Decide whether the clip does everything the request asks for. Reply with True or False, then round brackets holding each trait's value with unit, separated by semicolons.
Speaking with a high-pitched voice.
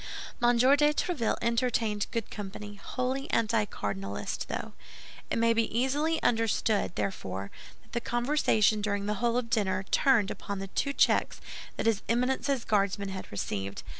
True (225 Hz)